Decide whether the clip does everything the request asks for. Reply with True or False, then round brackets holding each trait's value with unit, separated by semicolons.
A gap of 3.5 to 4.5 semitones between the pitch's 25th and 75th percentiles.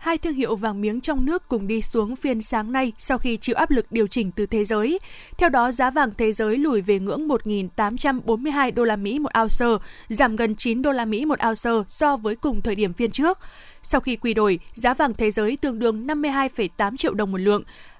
True (4.1 semitones)